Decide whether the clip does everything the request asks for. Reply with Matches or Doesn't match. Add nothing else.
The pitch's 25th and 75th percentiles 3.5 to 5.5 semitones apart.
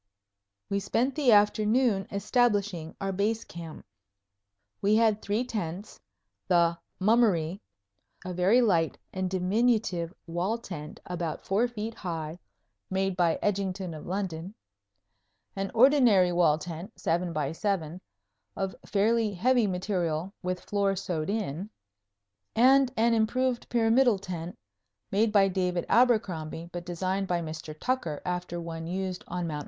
Matches